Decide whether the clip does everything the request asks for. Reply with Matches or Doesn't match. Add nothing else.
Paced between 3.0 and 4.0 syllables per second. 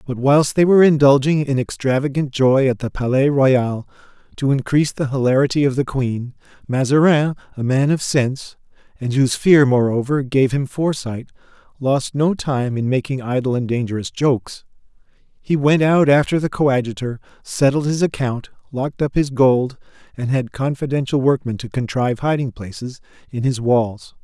Doesn't match